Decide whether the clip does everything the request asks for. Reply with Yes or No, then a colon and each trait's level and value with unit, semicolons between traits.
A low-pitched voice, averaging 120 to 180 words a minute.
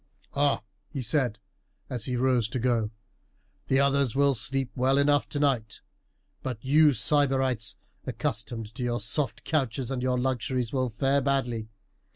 Yes: low, 130 Hz; average, 145 wpm